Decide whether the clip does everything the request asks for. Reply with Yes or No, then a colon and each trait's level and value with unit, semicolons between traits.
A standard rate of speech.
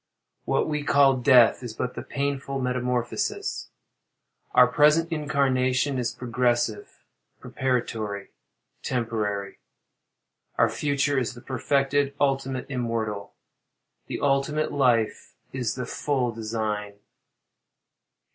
No: slow, 95 wpm